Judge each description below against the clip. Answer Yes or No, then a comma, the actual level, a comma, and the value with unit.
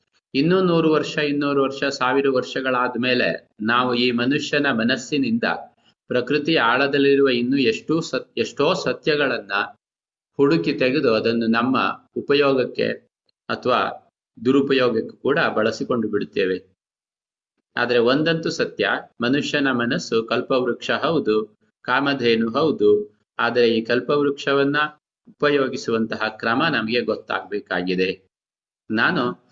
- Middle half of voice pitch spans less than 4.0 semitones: Yes, average, 3.6 semitones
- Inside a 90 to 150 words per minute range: Yes, average, 95 wpm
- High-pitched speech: No, low, 130 Hz